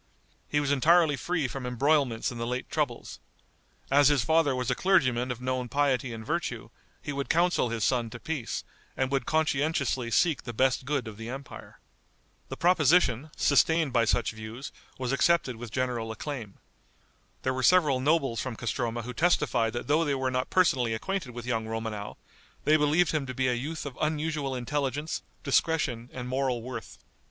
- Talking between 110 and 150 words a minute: No, average, 180 wpm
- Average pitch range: Yes, average, 3.8 semitones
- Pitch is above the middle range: No, low, 130 Hz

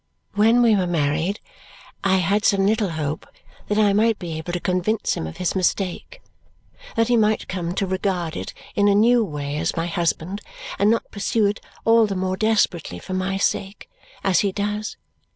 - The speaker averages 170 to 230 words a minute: Yes, average, 190 wpm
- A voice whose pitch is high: Yes, high, 195 Hz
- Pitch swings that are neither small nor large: Yes, average, 3.4 semitones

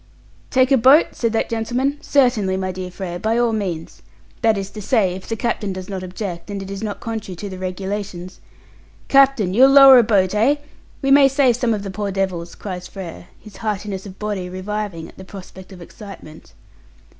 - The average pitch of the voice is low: No, high, 205 Hz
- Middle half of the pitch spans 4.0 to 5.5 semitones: No, average, 3.6 semitones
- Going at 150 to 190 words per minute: No, average, 200 wpm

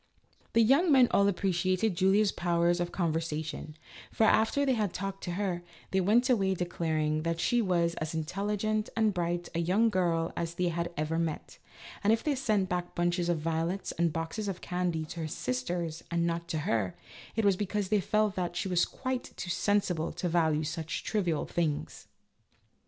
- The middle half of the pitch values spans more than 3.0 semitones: Yes, average, 3.5 semitones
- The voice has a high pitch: No, medium, 175 Hz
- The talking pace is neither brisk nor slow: Yes, average, 180 wpm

